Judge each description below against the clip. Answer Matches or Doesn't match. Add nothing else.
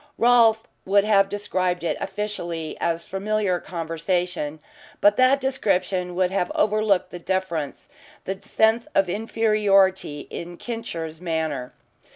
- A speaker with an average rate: Doesn't match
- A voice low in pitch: Doesn't match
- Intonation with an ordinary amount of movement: Matches